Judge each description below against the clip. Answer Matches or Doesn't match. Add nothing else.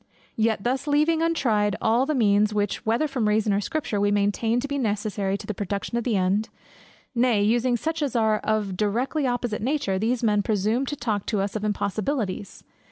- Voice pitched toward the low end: Doesn't match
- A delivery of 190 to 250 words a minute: Matches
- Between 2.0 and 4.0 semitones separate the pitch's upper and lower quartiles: Matches